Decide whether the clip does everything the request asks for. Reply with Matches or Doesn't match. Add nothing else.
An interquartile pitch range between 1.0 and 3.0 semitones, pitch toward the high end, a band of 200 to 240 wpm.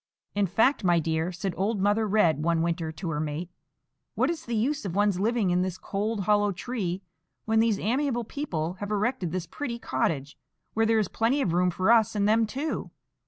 Doesn't match